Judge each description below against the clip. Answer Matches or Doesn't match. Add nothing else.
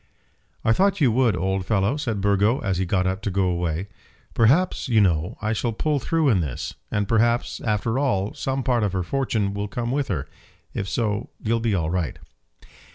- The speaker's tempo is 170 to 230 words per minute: Matches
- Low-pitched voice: Matches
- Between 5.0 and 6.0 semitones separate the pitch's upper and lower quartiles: Doesn't match